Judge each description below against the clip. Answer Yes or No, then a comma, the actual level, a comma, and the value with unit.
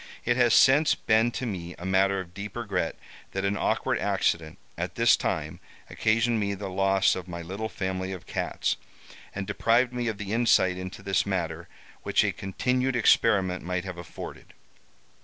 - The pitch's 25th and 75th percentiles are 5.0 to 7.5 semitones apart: No, average, 3.6 semitones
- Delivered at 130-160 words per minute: No, average, 175 wpm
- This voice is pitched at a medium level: No, very low, 95 Hz